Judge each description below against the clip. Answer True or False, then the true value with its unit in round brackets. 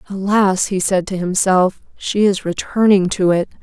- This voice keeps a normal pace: True (165 wpm)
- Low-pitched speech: False (190 Hz)